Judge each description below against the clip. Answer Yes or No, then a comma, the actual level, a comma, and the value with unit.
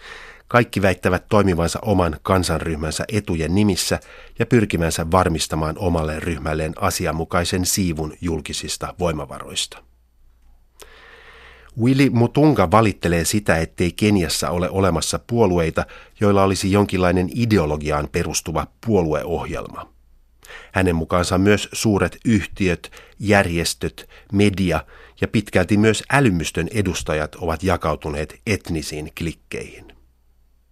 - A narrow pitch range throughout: No, average, 4.3 semitones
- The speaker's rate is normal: No, slow, 90 wpm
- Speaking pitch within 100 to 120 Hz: No, very low, 90 Hz